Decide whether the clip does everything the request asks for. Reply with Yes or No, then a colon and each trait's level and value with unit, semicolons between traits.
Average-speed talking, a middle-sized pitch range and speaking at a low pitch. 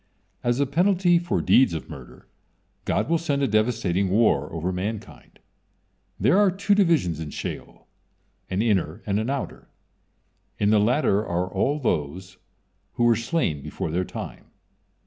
No: average, 150 wpm; wide, 7.9 semitones; low, 110 Hz